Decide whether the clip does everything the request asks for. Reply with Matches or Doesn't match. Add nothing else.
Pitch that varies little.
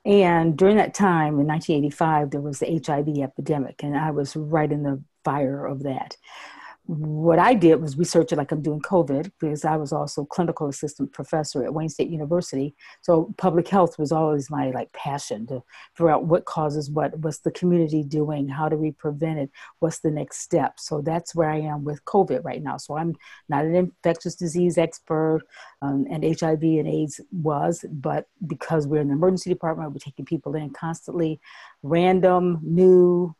Matches